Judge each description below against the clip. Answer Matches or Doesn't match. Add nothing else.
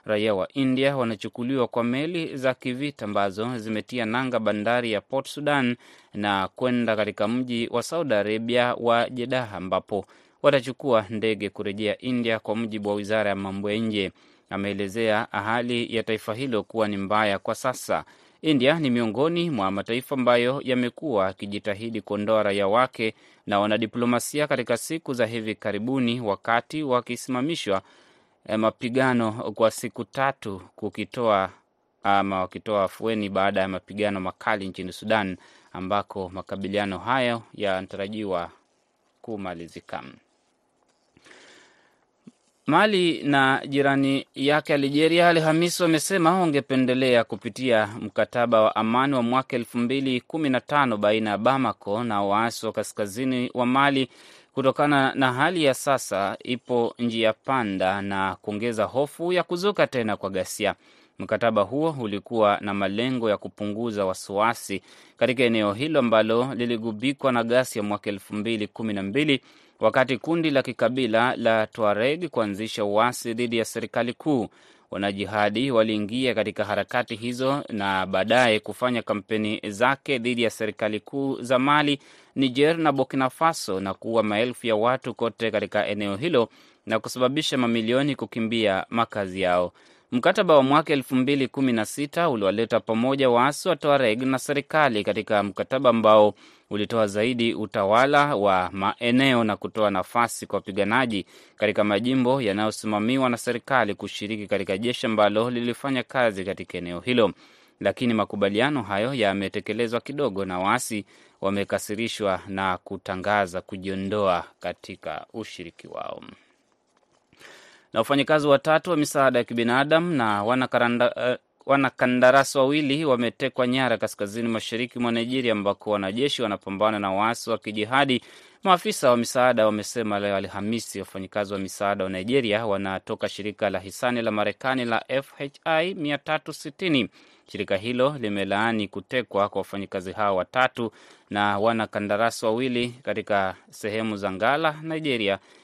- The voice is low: Matches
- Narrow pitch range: Doesn't match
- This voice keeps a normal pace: Matches